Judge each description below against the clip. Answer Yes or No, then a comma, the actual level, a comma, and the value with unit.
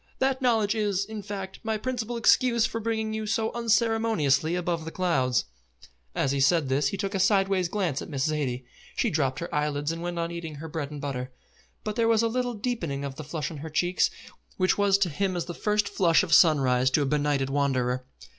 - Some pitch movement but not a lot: No, wide, 6.8 semitones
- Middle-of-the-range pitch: Yes, medium, 175 Hz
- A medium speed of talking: No, fast, 215 wpm